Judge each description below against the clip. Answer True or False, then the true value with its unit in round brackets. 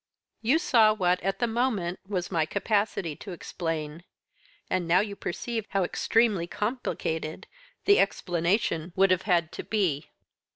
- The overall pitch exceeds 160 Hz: True (190 Hz)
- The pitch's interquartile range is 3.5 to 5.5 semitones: True (4.0 semitones)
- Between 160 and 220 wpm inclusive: False (140 wpm)